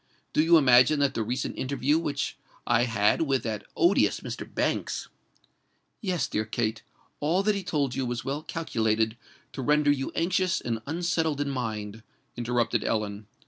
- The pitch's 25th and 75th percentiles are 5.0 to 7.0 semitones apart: Yes, wide, 5.4 semitones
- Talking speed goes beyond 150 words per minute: Yes, average, 160 wpm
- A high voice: No, low, 135 Hz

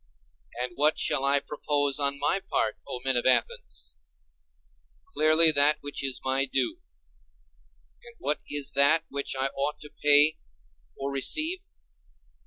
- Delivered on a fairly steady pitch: Yes, narrow, 1.9 semitones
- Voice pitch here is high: No, medium, 140 Hz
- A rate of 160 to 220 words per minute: No, average, 145 wpm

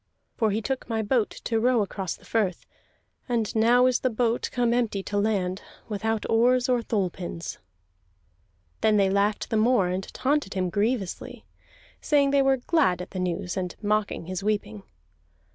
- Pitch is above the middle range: Yes, high, 215 Hz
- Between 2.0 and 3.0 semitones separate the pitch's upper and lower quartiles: No, average, 4.0 semitones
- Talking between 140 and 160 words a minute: No, average, 170 wpm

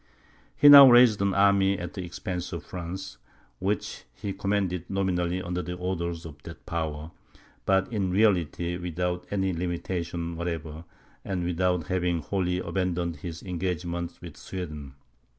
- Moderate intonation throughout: No, narrow, 2.0 semitones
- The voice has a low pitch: Yes, very low, 90 Hz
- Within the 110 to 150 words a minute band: Yes, average, 140 wpm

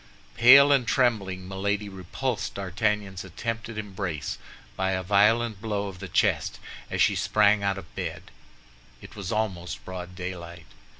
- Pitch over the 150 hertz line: No, low, 100 Hz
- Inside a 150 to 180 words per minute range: No, average, 140 wpm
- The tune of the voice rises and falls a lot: No, average, 2.8 semitones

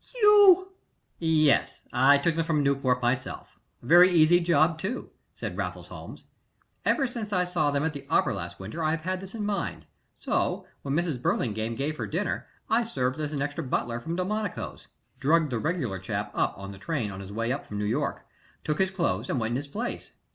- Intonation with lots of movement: Yes, wide, 6.1 semitones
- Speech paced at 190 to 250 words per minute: Yes, fast, 205 wpm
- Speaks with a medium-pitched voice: Yes, medium, 155 Hz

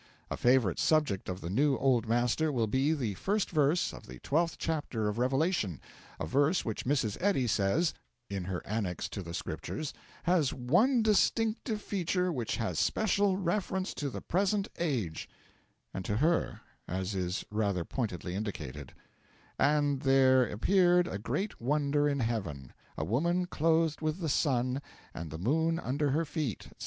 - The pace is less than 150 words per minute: No, average, 160 wpm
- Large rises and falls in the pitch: Yes, wide, 7.8 semitones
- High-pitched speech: No, low, 135 Hz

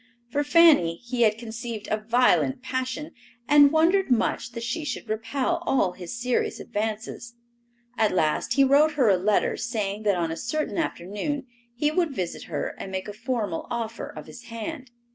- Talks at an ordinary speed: Yes, average, 175 wpm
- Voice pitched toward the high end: Yes, high, 235 Hz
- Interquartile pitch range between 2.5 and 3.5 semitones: No, average, 4.6 semitones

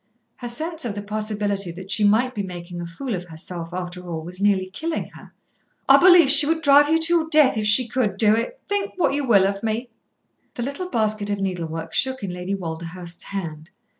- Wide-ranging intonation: Yes, wide, 6.8 semitones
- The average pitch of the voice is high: Yes, high, 205 Hz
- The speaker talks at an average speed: No, fast, 215 wpm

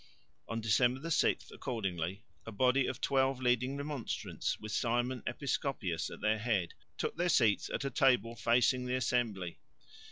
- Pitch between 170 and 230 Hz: No, low, 120 Hz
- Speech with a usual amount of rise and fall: Yes, average, 3.4 semitones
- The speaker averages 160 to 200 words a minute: No, average, 150 wpm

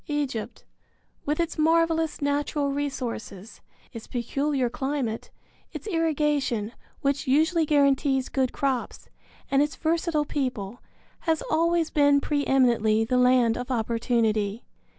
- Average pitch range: Yes, average, 3.9 semitones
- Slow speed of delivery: Yes, slow, 115 wpm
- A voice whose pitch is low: No, very high, 275 Hz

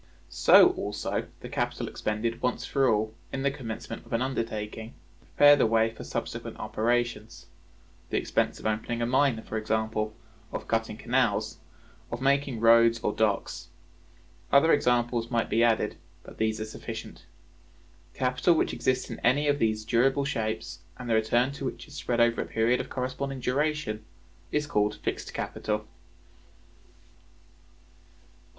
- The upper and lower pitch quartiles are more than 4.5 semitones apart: No, average, 3.0 semitones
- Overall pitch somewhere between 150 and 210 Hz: No, low, 115 Hz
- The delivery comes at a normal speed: Yes, average, 150 wpm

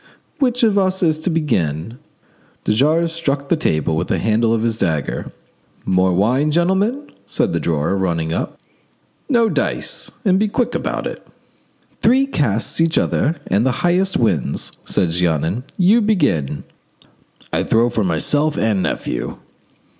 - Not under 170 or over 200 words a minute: No, average, 145 wpm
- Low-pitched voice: Yes, low, 130 Hz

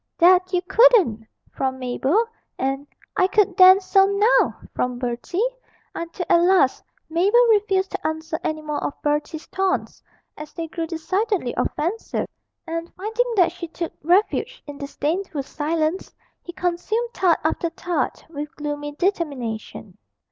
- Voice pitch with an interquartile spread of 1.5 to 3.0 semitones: No, average, 4.4 semitones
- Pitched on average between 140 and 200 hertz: No, very high, 340 Hz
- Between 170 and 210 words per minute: No, average, 140 wpm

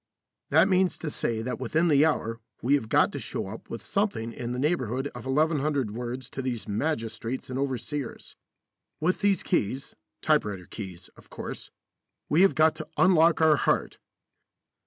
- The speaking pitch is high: No, low, 135 Hz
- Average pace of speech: Yes, average, 160 wpm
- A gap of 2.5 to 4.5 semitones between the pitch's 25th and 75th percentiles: No, wide, 5.4 semitones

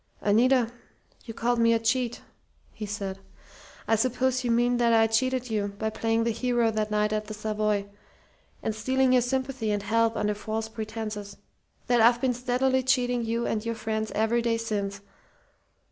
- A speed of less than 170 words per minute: No, average, 175 wpm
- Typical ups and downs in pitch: No, narrow, 2.2 semitones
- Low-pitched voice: No, high, 225 Hz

